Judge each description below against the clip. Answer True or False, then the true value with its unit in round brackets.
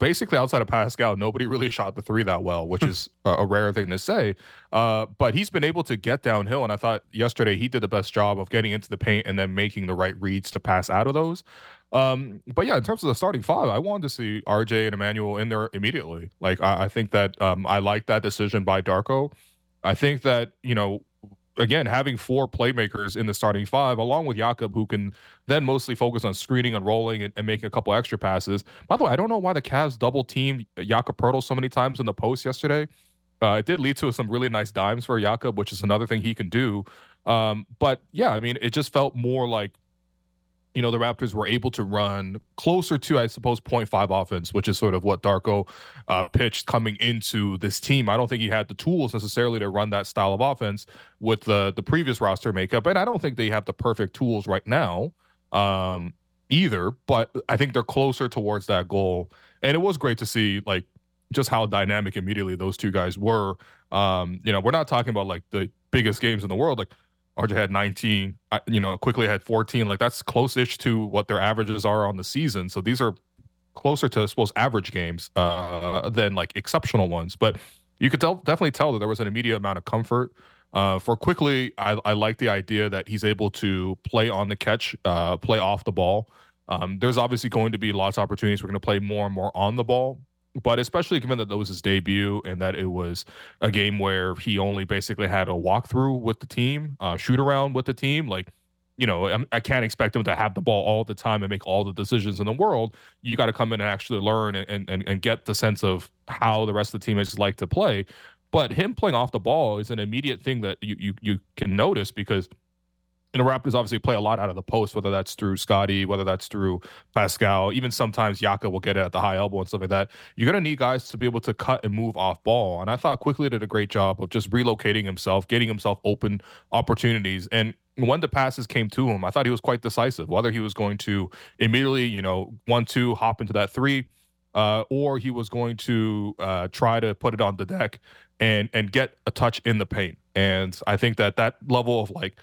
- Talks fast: True (235 wpm)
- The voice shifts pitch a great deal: False (3.5 semitones)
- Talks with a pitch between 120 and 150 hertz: False (110 Hz)